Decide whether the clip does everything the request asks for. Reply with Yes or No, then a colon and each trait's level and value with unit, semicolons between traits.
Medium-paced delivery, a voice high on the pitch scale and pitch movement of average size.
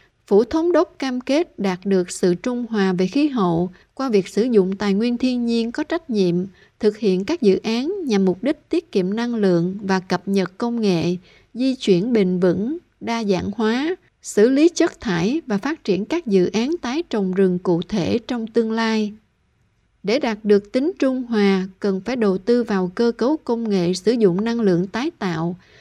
Yes: average, 200 wpm; high, 215 Hz; average, 4.7 semitones